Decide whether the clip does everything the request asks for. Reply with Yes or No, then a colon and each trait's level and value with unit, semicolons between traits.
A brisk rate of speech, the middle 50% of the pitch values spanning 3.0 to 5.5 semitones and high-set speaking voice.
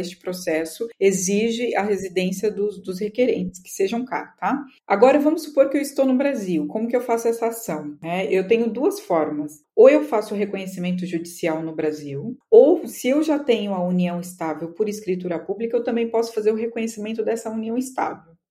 Yes: fast, 190 wpm; average, 4.9 semitones; high, 210 Hz